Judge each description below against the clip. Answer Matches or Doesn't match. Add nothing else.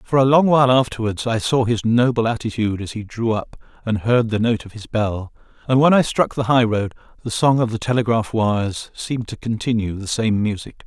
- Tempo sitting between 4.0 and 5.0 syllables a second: Doesn't match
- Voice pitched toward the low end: Matches